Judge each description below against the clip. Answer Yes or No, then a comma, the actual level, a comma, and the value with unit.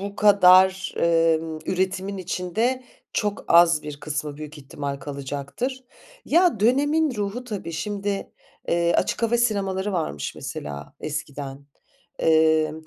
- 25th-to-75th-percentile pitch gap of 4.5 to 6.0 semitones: Yes, average, 5.3 semitones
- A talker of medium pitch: Yes, medium, 180 Hz